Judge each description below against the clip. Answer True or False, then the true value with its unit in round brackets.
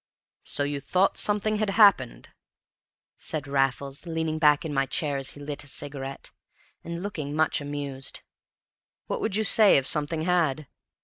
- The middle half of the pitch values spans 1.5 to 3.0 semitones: False (3.9 semitones)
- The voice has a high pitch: False (150 Hz)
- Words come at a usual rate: True (160 wpm)